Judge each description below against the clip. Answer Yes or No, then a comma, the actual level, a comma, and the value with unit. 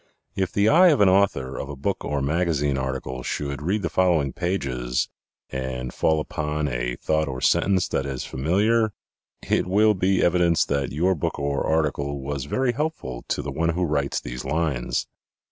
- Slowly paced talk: No, average, 180 wpm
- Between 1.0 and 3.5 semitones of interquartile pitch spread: No, wide, 5.4 semitones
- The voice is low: Yes, very low, 75 Hz